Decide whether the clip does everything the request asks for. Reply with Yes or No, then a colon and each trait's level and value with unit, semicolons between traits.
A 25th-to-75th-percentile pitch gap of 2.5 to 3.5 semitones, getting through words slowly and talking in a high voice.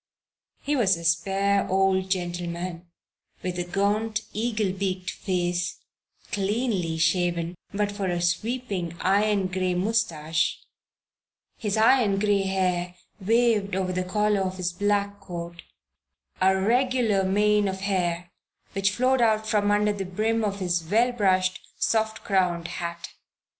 Yes: average, 2.8 semitones; slow, 130 wpm; high, 195 Hz